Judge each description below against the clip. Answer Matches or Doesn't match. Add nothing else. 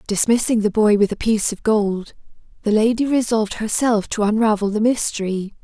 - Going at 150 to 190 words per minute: Matches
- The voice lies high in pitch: Matches